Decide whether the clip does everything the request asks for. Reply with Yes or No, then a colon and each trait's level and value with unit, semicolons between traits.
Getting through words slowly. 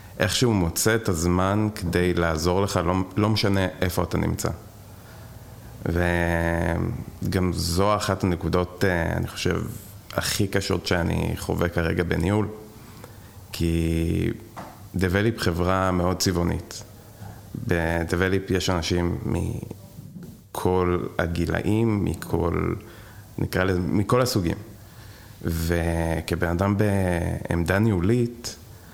Yes: slow, 95 wpm